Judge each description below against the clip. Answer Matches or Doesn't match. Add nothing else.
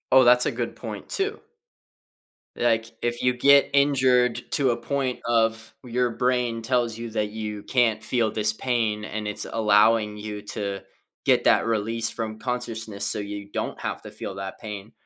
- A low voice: Matches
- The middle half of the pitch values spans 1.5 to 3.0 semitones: Matches